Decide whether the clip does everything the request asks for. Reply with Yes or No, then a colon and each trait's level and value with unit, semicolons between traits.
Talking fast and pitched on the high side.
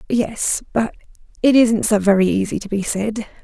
No: average, 155 wpm; high, 215 Hz